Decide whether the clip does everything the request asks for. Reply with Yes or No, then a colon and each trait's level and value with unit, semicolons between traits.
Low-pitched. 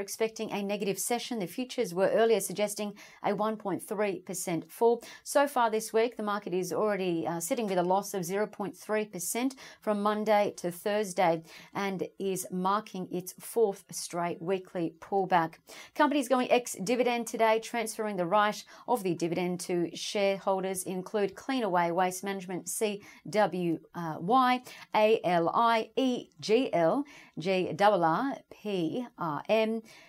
No: high, 200 Hz